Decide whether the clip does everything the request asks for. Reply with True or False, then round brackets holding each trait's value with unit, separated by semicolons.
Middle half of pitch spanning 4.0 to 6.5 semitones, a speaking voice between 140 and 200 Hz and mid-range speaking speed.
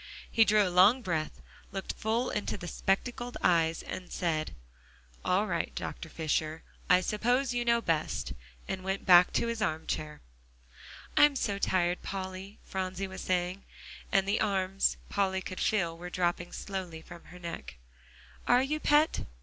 False (3.5 semitones; 190 Hz; 155 wpm)